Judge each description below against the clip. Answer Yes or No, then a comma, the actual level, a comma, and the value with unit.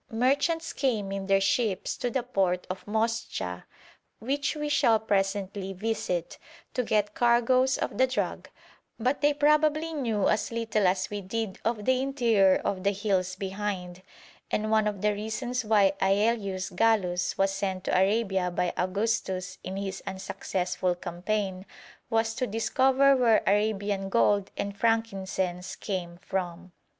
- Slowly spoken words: No, average, 145 wpm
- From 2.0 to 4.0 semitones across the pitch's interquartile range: Yes, average, 3.3 semitones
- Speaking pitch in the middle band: No, high, 205 Hz